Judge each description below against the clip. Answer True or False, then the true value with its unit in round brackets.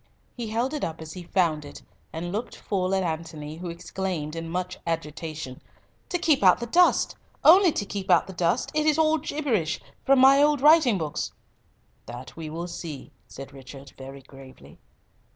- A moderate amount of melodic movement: False (8.2 semitones)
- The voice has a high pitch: False (175 Hz)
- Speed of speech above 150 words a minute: True (175 wpm)